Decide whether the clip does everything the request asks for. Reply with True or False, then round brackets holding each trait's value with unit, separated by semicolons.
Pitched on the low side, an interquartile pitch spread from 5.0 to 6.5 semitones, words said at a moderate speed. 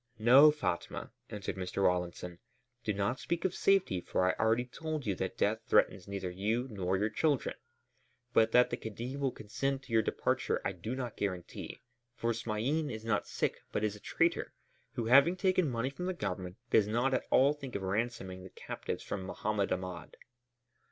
True (110 Hz; 5.5 semitones; 185 wpm)